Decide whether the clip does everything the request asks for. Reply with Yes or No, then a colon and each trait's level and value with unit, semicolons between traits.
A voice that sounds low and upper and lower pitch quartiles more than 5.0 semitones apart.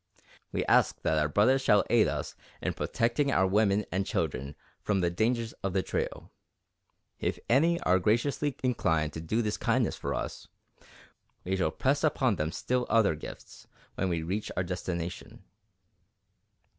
Yes: low, 100 Hz; wide, 5.5 semitones